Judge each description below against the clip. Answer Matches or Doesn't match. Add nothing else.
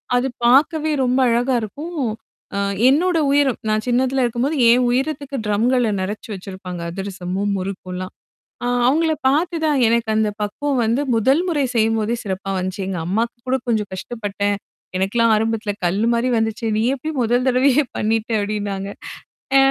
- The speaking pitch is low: Doesn't match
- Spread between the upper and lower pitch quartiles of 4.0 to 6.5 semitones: Matches